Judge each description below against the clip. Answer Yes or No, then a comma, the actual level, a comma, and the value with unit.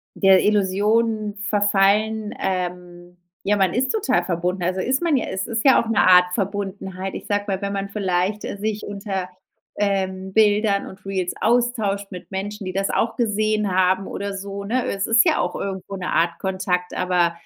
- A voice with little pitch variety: Yes, narrow, 2.2 semitones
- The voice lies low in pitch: No, high, 195 Hz